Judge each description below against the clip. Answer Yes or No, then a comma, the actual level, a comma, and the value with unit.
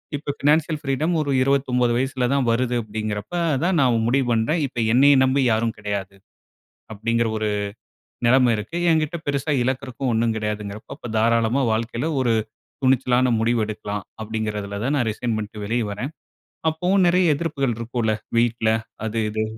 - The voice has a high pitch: No, low, 120 Hz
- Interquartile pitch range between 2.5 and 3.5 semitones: No, average, 3.9 semitones